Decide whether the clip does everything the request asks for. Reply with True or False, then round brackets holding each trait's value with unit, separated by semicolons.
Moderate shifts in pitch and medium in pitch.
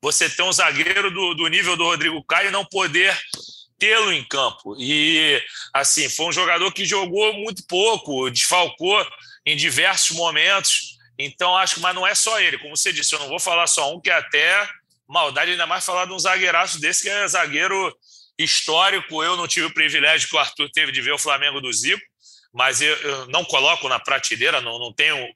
True (4.4 semitones; 175 Hz)